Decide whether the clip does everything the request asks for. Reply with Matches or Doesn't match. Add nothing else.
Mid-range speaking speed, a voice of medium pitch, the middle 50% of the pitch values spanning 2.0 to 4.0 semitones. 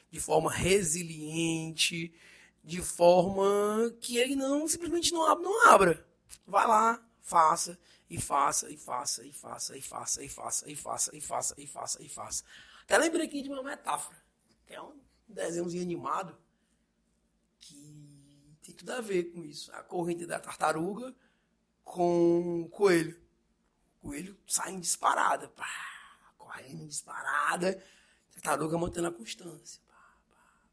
Doesn't match